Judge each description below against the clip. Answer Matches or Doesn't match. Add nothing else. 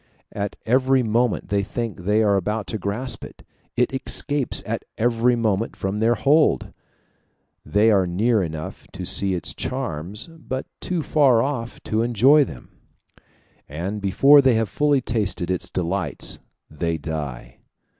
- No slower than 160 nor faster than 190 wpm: Doesn't match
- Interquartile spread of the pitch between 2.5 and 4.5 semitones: Doesn't match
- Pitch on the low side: Matches